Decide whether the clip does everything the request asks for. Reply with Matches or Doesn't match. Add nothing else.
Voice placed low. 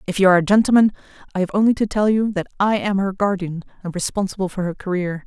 Doesn't match